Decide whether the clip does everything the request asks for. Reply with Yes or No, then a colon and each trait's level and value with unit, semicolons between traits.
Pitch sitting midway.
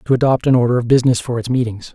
No: low, 125 Hz